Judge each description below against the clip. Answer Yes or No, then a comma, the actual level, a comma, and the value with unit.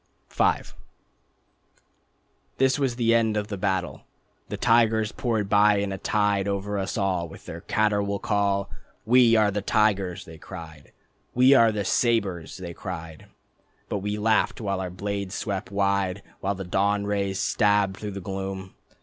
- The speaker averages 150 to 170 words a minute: Yes, average, 160 wpm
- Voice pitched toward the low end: Yes, low, 100 Hz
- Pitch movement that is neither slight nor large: No, narrow, 1.8 semitones